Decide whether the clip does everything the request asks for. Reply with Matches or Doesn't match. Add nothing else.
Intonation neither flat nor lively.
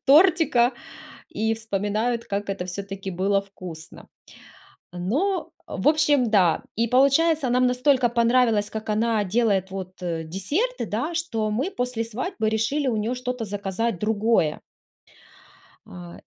Matches